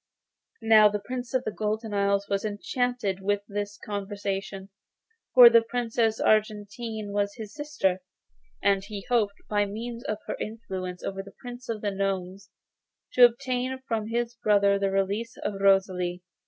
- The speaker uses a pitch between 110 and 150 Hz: No, high, 205 Hz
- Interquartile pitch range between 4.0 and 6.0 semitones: No, average, 2.7 semitones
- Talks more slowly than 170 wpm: Yes, average, 155 wpm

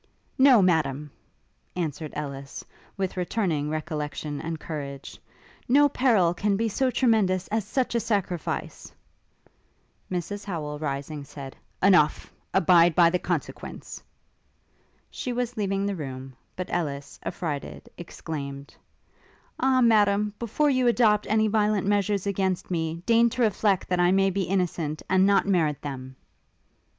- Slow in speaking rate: Yes, slow, 130 wpm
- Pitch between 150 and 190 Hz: Yes, medium, 185 Hz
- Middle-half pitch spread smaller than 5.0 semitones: No, wide, 5.5 semitones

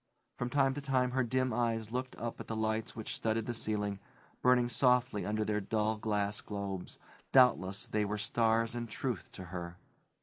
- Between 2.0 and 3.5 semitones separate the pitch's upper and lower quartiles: Yes, average, 2.9 semitones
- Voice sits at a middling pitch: No, low, 110 Hz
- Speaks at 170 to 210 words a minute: Yes, average, 180 wpm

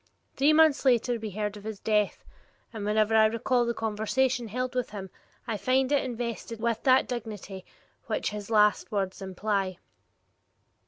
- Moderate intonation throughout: Yes, average, 3.0 semitones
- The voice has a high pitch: Yes, high, 220 Hz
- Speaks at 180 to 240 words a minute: No, average, 155 wpm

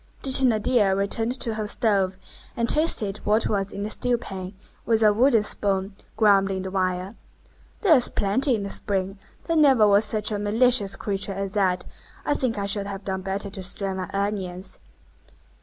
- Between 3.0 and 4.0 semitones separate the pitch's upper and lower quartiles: No, narrow, 2.6 semitones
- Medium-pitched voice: No, high, 205 Hz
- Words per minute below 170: No, average, 175 wpm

